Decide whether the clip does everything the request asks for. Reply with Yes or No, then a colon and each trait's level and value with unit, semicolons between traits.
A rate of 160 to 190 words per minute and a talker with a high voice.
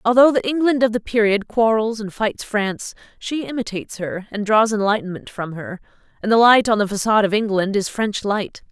No: average, 200 wpm; high, 215 Hz